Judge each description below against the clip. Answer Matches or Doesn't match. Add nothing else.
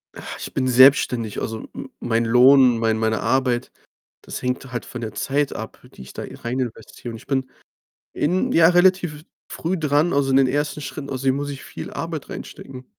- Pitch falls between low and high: Doesn't match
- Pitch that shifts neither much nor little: Matches